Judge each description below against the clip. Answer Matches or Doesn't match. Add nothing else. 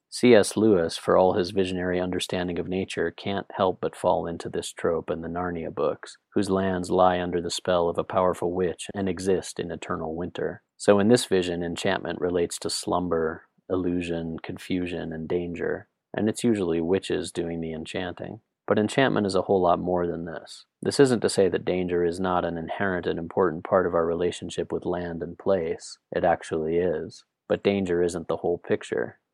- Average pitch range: Doesn't match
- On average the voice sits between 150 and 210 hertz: Doesn't match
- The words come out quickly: Doesn't match